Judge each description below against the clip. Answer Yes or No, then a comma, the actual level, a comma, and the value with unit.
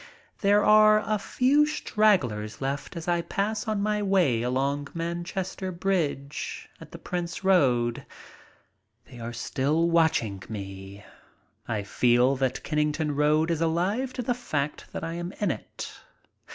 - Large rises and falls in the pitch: Yes, wide, 6.9 semitones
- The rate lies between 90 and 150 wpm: Yes, average, 140 wpm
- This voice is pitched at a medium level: Yes, medium, 165 Hz